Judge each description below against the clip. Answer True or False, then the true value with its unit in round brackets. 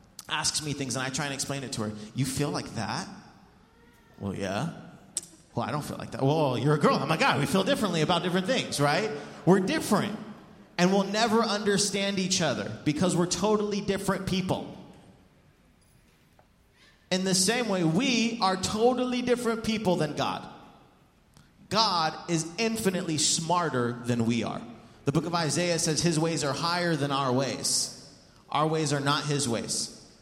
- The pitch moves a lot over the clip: True (6.1 semitones)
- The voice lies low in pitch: False (165 Hz)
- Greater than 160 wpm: True (175 wpm)